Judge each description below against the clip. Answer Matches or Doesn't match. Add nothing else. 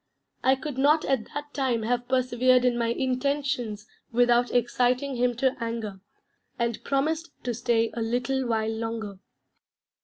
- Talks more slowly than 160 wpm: Matches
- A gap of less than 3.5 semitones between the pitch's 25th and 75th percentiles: Matches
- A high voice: Matches